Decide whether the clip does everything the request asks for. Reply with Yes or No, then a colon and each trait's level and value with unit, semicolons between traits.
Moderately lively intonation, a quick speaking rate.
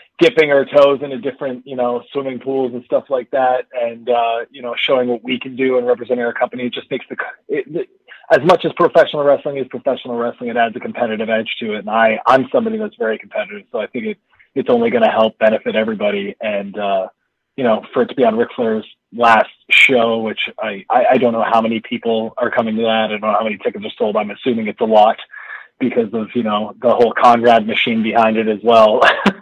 Yes: average, 3.9 semitones; fast, 235 wpm